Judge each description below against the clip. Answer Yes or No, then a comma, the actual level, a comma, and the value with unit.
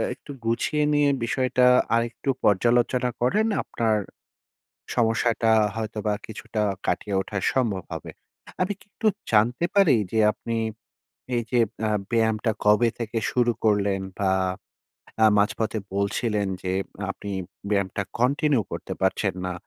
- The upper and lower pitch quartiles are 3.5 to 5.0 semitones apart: No, average, 2.8 semitones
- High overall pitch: No, low, 115 Hz